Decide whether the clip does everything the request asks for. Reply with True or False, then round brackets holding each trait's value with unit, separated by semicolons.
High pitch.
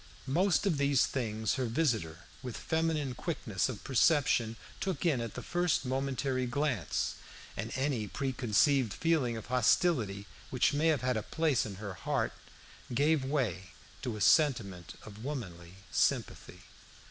False (130 Hz)